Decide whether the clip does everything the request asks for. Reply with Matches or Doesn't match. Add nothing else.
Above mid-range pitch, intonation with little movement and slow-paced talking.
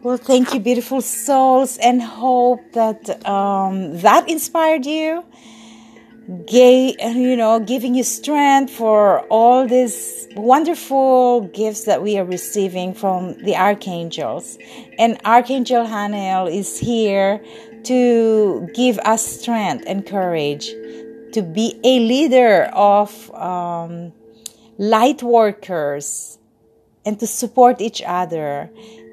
Doesn't match